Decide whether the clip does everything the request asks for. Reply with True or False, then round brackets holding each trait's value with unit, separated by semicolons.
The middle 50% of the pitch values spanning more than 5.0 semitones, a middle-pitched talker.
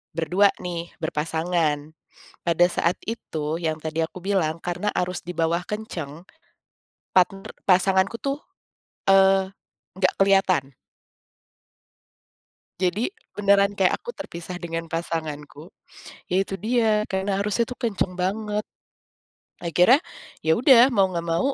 False (3.2 semitones; 180 Hz)